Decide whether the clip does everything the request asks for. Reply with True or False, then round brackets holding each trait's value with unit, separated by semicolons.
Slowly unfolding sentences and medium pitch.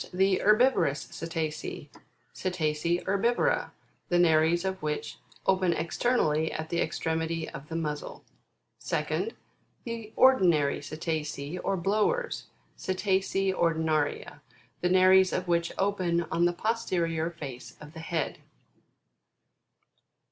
True (110 wpm; 170 Hz)